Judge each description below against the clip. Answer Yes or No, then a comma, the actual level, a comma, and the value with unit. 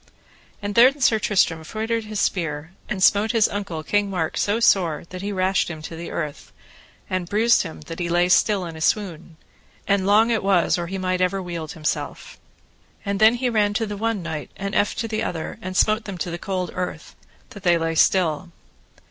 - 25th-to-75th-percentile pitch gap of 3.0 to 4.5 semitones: Yes, average, 3.5 semitones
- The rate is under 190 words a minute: No, fast, 205 wpm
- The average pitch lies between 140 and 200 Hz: Yes, high, 190 Hz